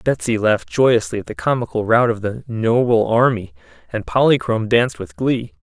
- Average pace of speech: Yes, average, 170 wpm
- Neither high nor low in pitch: No, low, 110 Hz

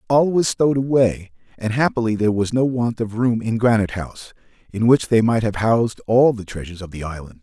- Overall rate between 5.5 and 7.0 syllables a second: Yes, 6.0 syllables/s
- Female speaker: No, male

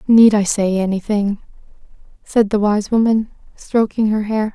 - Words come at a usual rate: Yes, average, 160 wpm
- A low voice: No, high, 210 Hz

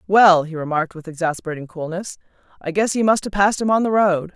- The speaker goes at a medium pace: No, fast, 220 wpm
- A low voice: No, medium, 185 Hz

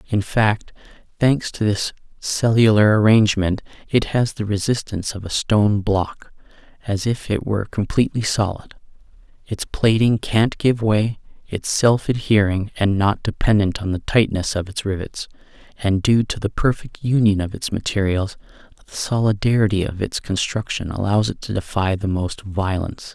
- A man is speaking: Yes, male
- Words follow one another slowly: No, average, 155 wpm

